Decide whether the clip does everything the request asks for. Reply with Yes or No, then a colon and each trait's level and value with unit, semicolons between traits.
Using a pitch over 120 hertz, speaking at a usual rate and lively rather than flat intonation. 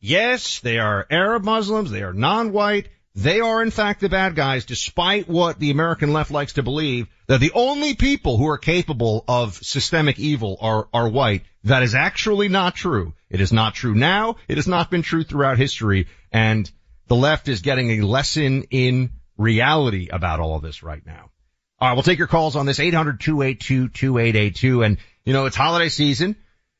Yes: low, 135 Hz; average, 185 wpm; wide, 7.0 semitones